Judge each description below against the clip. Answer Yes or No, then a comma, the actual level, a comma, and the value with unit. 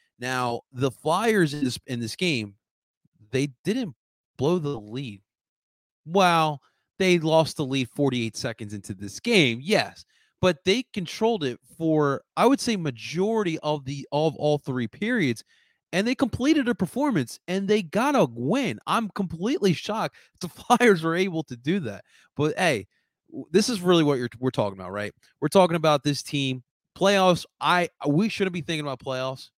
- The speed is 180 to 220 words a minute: No, average, 170 wpm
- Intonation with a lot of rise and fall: Yes, wide, 6.9 semitones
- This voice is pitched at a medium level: Yes, medium, 155 Hz